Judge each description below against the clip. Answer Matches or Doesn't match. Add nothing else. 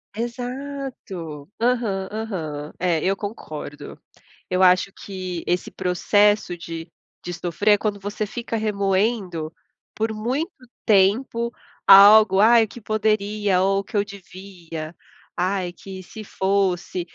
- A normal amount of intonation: Matches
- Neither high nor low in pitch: Doesn't match